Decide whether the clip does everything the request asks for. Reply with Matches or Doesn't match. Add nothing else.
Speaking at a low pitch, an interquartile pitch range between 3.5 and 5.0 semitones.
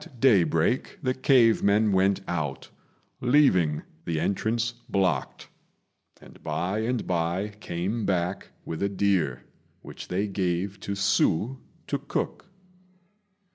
Matches